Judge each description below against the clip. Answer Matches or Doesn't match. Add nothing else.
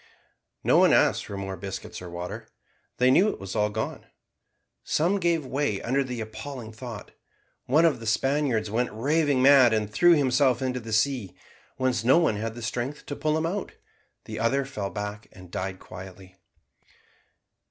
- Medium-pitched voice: Doesn't match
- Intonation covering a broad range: Doesn't match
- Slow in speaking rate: Doesn't match